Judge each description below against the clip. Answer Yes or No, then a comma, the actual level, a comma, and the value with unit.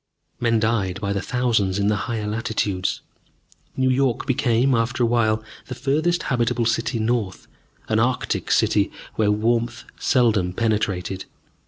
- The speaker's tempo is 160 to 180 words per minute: No, slow, 135 wpm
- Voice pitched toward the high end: No, low, 115 Hz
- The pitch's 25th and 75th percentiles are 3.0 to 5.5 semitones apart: No, narrow, 2.6 semitones